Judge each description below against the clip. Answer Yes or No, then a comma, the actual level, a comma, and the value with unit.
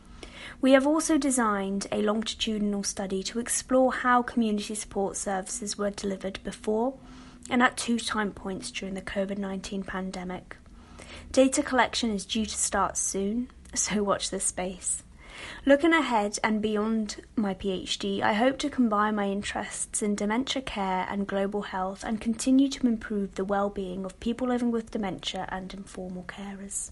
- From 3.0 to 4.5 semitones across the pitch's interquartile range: Yes, average, 3.5 semitones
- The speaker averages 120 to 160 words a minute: Yes, average, 155 wpm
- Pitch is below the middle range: No, high, 210 Hz